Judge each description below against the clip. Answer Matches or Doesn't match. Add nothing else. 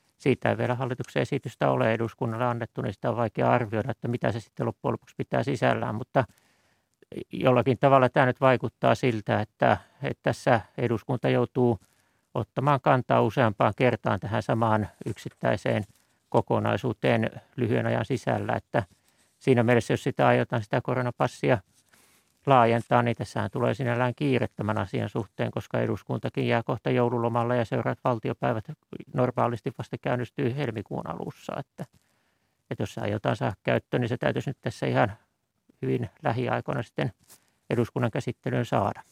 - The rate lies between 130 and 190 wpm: Matches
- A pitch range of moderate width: Doesn't match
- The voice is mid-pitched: Doesn't match